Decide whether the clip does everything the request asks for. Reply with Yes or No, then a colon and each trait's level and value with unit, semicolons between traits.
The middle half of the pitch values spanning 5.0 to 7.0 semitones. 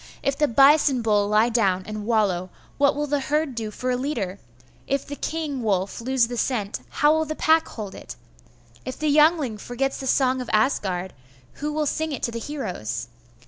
Yes: wide, 5.4 semitones